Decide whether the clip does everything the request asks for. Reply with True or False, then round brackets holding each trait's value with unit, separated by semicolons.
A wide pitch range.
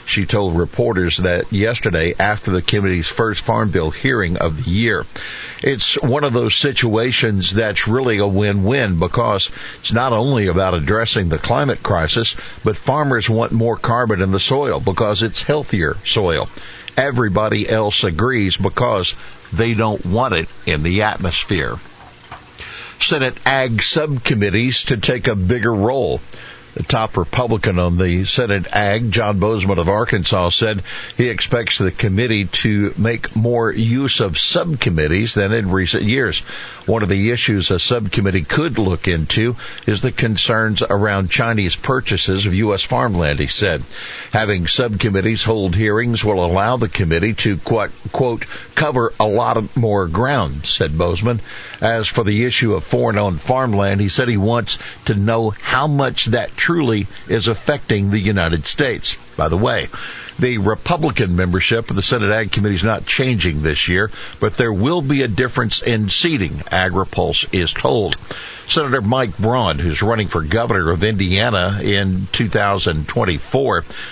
False (3.5 semitones)